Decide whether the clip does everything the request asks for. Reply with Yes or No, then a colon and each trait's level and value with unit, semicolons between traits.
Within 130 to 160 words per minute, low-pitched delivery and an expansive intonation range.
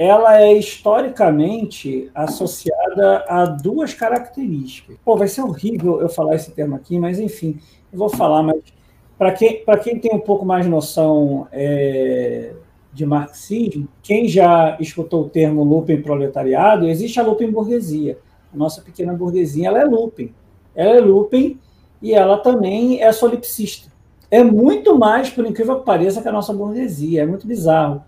No: average, 155 wpm; medium, 185 Hz; wide, 6.3 semitones